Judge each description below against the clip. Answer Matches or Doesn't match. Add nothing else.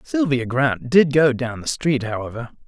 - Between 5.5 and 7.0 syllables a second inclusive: Doesn't match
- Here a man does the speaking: Matches